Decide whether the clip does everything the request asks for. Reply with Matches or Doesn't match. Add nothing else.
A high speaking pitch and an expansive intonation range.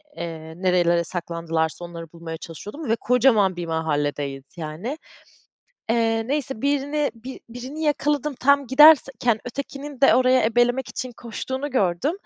Matches